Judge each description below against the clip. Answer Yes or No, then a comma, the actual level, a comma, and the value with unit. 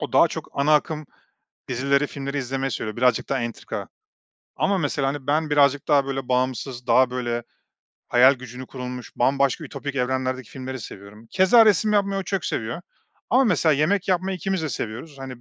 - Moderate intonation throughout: Yes, average, 3.7 semitones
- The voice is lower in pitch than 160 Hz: Yes, low, 135 Hz